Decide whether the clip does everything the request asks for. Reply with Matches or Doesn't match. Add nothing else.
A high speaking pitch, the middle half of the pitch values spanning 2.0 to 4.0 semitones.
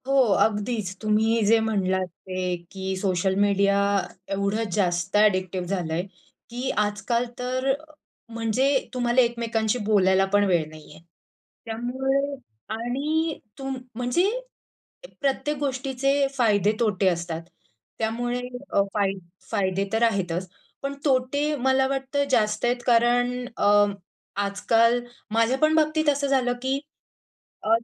Doesn't match